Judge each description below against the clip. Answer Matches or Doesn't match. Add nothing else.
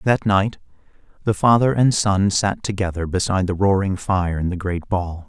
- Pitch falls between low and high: Doesn't match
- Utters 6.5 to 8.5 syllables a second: Doesn't match